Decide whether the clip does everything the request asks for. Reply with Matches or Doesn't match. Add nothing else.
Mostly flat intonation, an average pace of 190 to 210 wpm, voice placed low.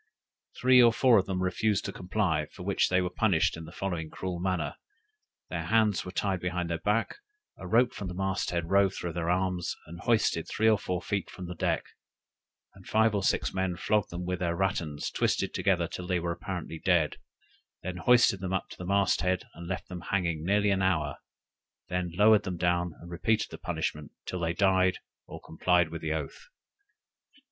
Matches